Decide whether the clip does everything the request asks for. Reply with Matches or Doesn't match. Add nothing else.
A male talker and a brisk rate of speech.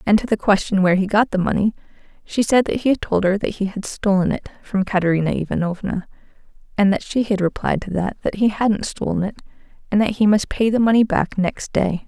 Doesn't match